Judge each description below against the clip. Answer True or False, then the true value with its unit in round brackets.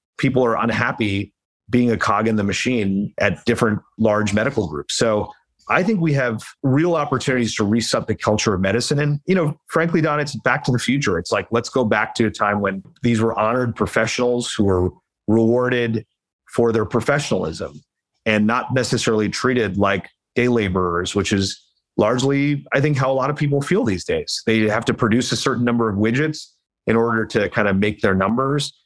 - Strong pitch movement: False (3.9 semitones)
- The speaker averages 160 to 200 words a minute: True (195 wpm)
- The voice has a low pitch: True (115 Hz)